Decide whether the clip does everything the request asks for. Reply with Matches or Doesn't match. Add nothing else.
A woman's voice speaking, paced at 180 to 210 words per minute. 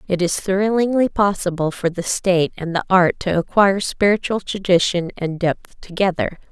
Doesn't match